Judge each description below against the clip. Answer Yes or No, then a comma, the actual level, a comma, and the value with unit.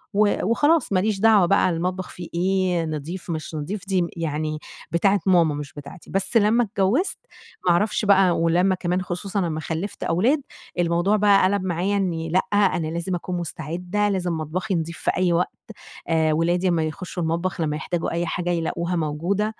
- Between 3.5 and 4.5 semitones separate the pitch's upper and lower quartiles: No, average, 2.9 semitones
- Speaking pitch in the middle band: Yes, medium, 180 Hz